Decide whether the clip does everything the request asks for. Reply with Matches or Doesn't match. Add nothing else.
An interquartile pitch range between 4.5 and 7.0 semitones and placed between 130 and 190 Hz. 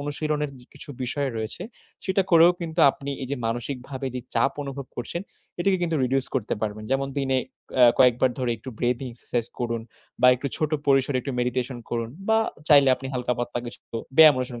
Doesn't match